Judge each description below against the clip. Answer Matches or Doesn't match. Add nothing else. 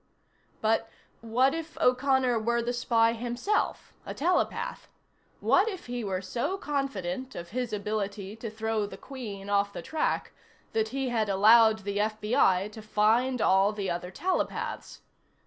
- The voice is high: Matches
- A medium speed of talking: Matches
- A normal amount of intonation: Matches